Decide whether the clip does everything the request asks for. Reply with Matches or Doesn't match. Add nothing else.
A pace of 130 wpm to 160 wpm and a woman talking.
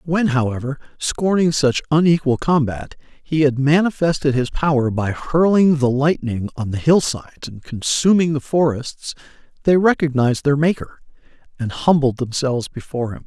Doesn't match